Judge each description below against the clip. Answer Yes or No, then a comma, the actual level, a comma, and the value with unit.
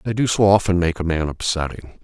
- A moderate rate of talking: No, fast, 235 wpm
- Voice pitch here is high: No, very low, 90 Hz